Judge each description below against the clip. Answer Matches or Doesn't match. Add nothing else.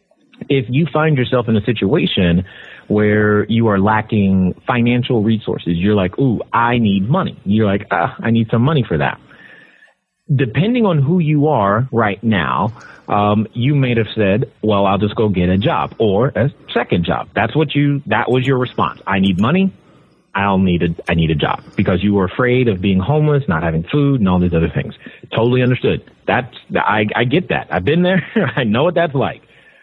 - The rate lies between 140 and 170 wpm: Doesn't match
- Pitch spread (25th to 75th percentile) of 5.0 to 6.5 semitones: Matches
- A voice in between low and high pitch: Doesn't match